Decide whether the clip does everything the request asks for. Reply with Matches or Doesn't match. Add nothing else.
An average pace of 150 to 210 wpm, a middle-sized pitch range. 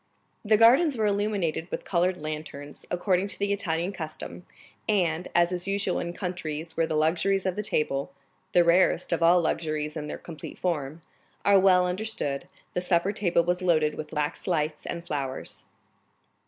Matches